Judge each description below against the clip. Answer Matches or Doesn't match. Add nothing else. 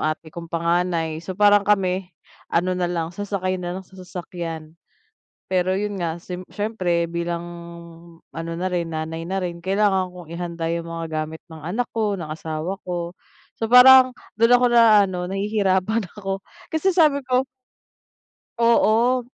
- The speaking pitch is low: Doesn't match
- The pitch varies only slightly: Doesn't match